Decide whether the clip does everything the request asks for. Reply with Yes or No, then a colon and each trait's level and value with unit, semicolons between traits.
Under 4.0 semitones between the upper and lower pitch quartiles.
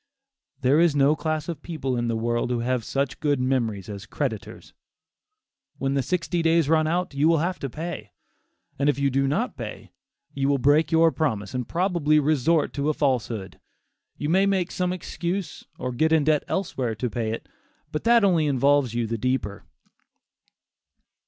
No: average, 4.5 semitones